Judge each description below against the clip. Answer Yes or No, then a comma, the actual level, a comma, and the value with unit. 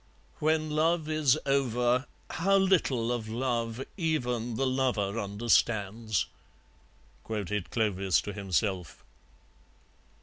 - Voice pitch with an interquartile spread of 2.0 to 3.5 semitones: No, average, 5.0 semitones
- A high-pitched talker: No, low, 120 Hz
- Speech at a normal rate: No, slow, 95 wpm